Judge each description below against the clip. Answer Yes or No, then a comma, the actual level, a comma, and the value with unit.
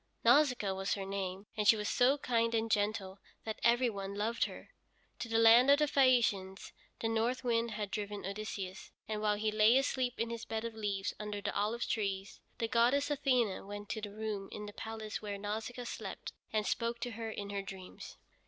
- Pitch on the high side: Yes, high, 220 Hz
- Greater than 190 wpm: Yes, average, 200 wpm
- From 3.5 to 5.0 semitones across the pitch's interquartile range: No, narrow, 2.4 semitones